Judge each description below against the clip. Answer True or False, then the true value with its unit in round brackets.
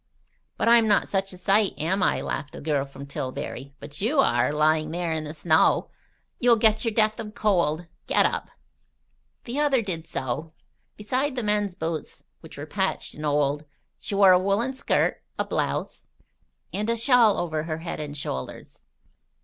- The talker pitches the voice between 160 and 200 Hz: True (185 Hz)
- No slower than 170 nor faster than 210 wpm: True (175 wpm)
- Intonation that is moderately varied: False (6.0 semitones)